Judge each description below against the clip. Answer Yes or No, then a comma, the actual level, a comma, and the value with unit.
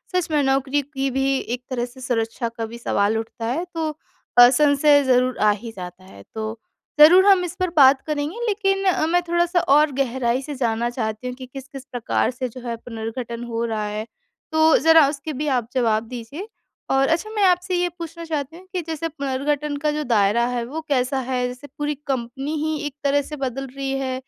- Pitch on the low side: No, very high, 270 Hz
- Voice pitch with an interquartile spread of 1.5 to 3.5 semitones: No, average, 4.2 semitones